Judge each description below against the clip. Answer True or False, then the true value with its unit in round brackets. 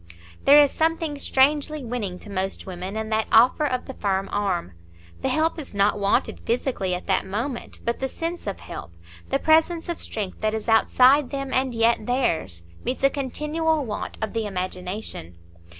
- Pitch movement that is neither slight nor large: False (6.1 semitones)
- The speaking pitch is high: True (235 Hz)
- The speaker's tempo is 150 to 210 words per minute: True (180 wpm)